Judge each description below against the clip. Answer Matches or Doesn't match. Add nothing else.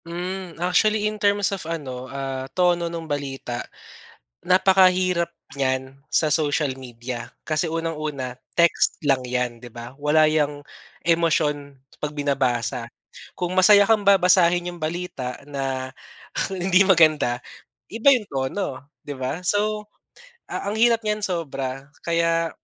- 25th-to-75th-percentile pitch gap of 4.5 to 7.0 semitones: Matches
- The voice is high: Doesn't match